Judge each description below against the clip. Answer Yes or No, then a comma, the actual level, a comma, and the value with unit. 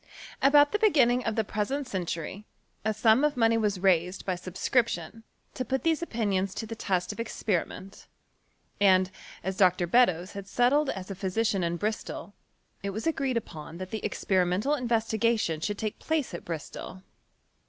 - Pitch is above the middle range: Yes, high, 210 Hz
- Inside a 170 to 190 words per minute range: Yes, average, 175 wpm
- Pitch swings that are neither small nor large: Yes, average, 4.5 semitones